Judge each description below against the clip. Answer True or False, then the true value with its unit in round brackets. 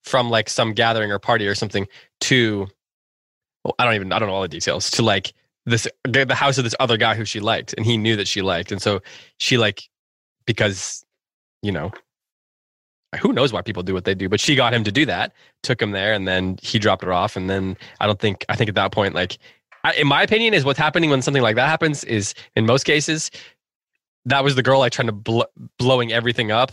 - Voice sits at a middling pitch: False (115 Hz)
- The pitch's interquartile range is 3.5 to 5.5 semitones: True (4.3 semitones)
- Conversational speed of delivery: False (240 wpm)